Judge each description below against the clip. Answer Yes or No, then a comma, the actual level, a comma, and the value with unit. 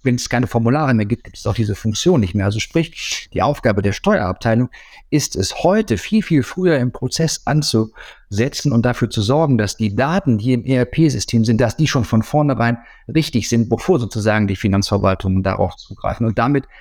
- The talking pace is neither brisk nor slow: No, fast, 195 wpm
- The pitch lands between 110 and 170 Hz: Yes, low, 120 Hz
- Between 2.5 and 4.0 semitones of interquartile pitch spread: No, average, 4.6 semitones